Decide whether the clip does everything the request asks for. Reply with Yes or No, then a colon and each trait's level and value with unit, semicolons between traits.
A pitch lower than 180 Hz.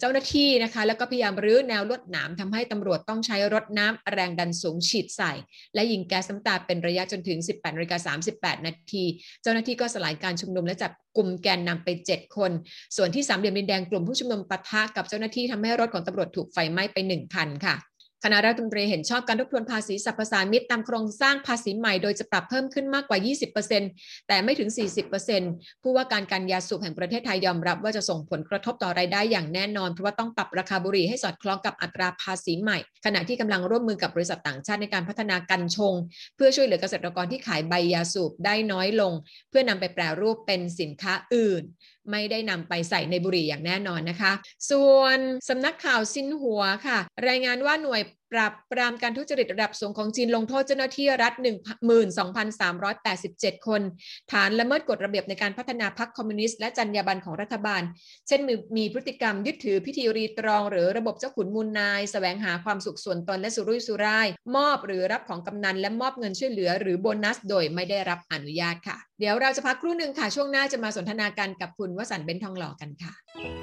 No: high, 205 Hz